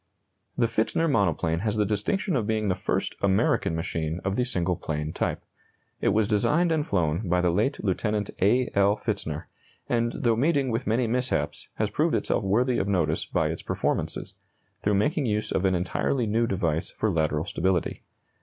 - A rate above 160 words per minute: Yes, average, 180 wpm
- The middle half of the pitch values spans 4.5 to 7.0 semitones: Yes, average, 4.9 semitones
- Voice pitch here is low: Yes, low, 105 Hz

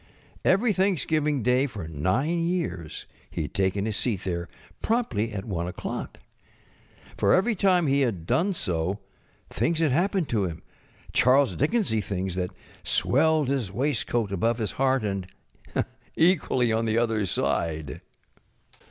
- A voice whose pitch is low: Yes, low, 120 Hz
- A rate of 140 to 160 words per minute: Yes, average, 145 wpm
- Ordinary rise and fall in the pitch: No, wide, 8.6 semitones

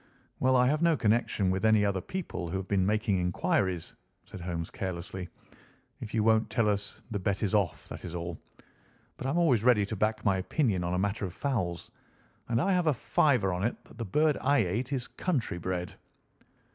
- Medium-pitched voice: No, low, 105 Hz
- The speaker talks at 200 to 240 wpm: Yes, fast, 205 wpm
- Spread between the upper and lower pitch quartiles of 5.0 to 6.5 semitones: Yes, average, 5.3 semitones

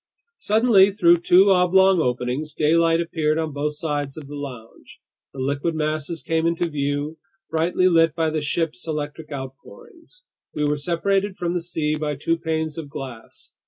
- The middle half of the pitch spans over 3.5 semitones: No, average, 2.8 semitones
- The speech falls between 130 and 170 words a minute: Yes, average, 160 wpm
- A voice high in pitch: No, medium, 160 Hz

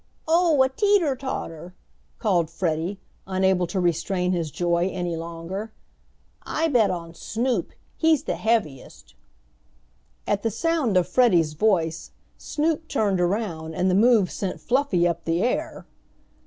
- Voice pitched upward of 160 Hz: Yes, high, 190 Hz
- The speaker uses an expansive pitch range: Yes, wide, 6.4 semitones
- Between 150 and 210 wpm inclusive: No, slow, 135 wpm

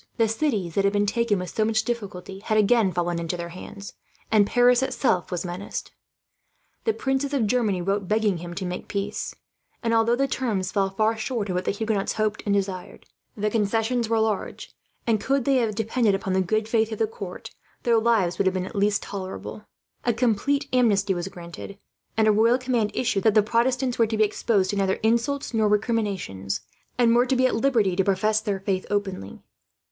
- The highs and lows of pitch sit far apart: No, average, 3.1 semitones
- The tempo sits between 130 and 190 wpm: No, fast, 205 wpm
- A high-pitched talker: Yes, high, 215 Hz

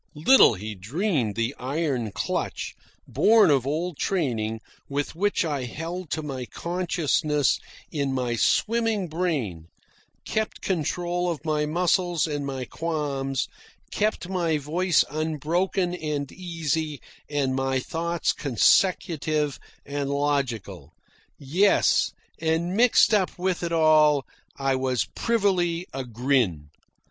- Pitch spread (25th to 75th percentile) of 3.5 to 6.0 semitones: Yes, average, 4.6 semitones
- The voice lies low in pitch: No, medium, 155 Hz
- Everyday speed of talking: No, slow, 115 wpm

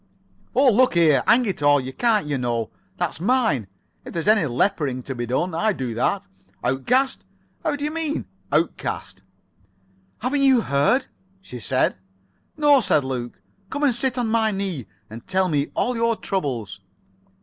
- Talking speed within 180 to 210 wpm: No, average, 165 wpm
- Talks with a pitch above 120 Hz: Yes, medium, 185 Hz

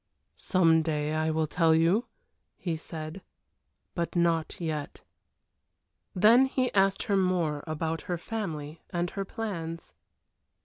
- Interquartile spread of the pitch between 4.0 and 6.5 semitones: No, average, 3.2 semitones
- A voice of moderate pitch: Yes, medium, 165 Hz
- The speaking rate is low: Yes, slow, 125 wpm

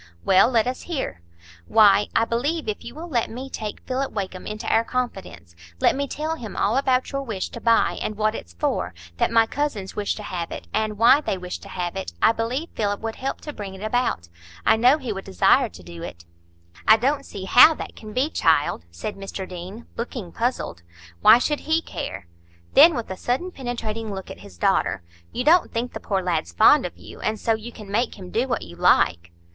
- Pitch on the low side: No, high, 220 Hz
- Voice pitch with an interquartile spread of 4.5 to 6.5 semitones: Yes, average, 5.2 semitones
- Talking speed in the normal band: No, fast, 215 wpm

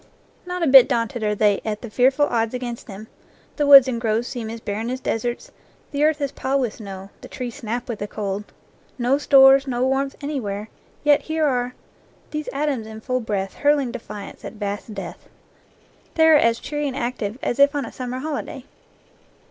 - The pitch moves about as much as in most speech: Yes, average, 4.1 semitones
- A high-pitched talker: Yes, high, 245 Hz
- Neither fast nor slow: Yes, average, 195 wpm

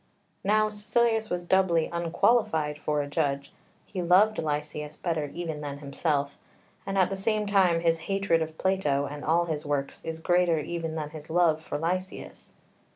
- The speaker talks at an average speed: Yes, average, 165 wpm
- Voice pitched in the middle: Yes, medium, 165 Hz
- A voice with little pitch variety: No, average, 4.1 semitones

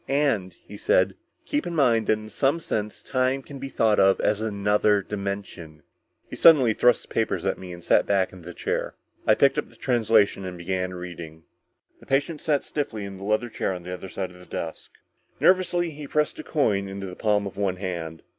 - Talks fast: Yes, fast, 210 wpm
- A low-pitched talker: Yes, low, 105 Hz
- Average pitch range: No, wide, 5.7 semitones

